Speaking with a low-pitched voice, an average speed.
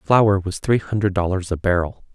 Yes: very low, 95 Hz; average, 195 wpm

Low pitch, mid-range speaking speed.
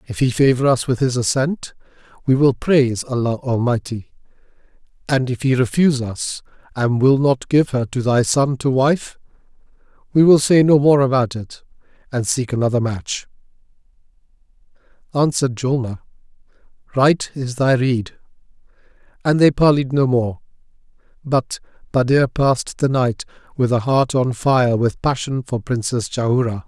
Yes: low, 130 Hz; average, 145 wpm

